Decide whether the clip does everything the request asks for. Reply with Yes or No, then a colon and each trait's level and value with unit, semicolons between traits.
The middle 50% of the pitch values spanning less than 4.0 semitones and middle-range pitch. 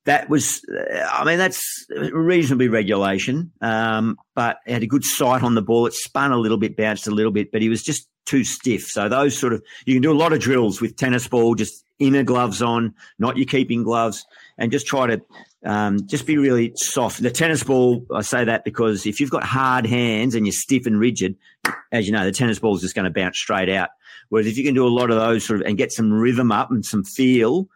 No: average, 3.0 semitones; low, 120 Hz